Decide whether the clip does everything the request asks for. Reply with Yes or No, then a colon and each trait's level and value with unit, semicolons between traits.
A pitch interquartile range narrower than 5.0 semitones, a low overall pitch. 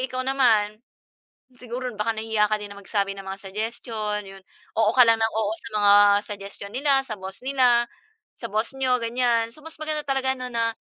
No: average, 3.4 semitones; high, 230 Hz